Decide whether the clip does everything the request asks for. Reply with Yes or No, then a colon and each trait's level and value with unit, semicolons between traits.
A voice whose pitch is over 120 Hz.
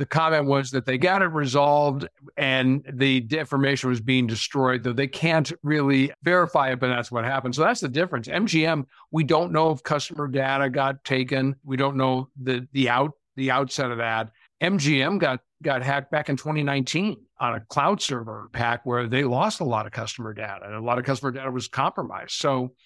Yes: low, 135 Hz